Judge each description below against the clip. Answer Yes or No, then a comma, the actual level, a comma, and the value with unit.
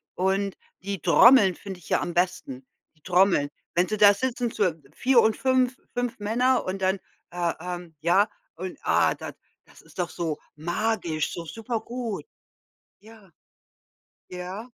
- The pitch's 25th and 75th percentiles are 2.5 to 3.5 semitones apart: No, average, 4.2 semitones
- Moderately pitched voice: No, high, 195 Hz